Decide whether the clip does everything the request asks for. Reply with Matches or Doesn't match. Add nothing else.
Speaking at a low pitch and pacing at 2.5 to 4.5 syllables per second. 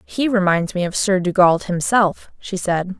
Doesn't match